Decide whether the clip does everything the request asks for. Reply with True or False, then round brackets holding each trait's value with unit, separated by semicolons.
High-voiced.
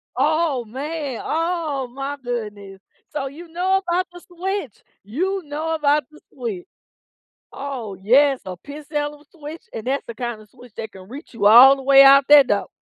True (275 Hz)